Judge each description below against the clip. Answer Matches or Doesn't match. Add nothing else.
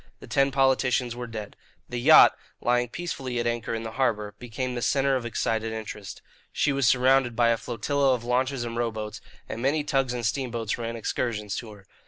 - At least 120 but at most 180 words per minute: Doesn't match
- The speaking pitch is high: Doesn't match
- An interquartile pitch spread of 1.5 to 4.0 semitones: Matches